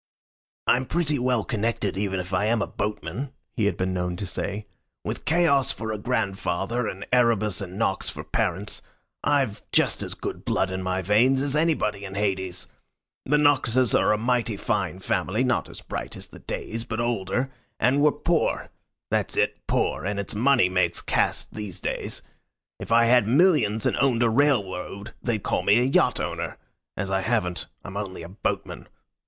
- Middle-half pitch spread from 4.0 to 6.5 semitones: Yes, average, 4.6 semitones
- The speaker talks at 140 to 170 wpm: No, average, 180 wpm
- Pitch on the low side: Yes, low, 110 Hz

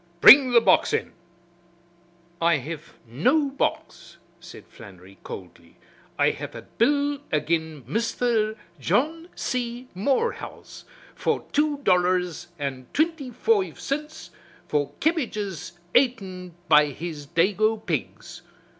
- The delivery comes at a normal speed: No, slow, 110 wpm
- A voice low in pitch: No, high, 205 Hz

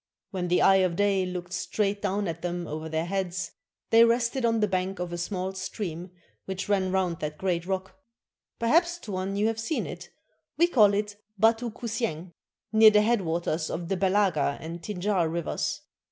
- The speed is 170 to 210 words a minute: Yes, average, 190 wpm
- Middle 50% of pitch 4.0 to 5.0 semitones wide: No, average, 3.2 semitones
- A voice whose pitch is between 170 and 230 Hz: Yes, high, 190 Hz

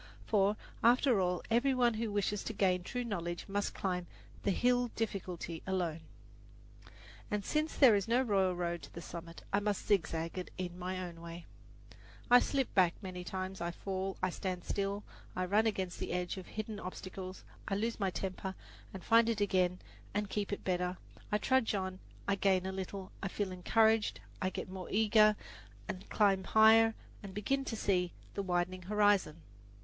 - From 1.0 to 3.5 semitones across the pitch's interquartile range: Yes, average, 2.7 semitones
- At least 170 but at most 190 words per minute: Yes, average, 180 wpm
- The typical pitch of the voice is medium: No, high, 195 Hz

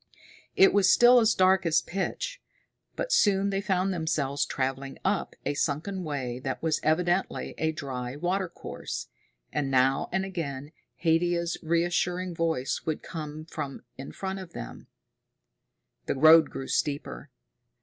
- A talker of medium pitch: Yes, medium, 165 Hz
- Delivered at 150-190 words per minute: No, average, 140 wpm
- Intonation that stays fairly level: No, average, 4.8 semitones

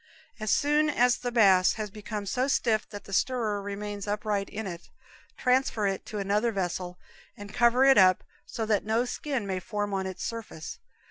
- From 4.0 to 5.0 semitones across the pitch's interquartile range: No, average, 3.2 semitones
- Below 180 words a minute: No, average, 185 wpm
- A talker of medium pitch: No, high, 210 Hz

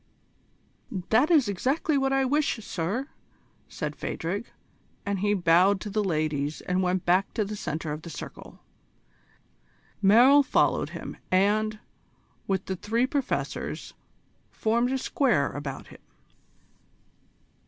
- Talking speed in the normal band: No, slow, 125 wpm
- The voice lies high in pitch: Yes, high, 205 Hz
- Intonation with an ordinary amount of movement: No, wide, 6.0 semitones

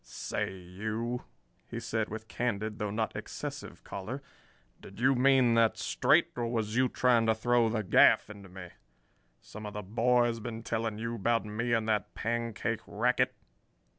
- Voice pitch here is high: No, low, 110 Hz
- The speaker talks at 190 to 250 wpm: No, average, 165 wpm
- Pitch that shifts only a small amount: Yes, narrow, 2.1 semitones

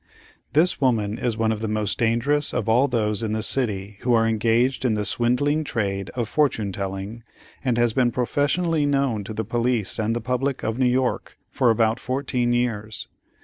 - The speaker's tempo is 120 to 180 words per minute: No, average, 190 wpm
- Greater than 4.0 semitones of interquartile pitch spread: No, average, 2.7 semitones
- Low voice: Yes, low, 120 Hz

